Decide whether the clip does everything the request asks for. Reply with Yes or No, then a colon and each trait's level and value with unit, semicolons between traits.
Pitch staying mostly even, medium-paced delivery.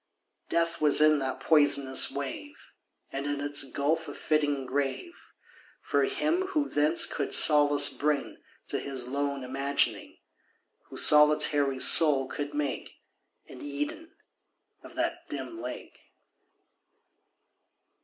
No: narrow, 1.7 semitones; slow, 115 wpm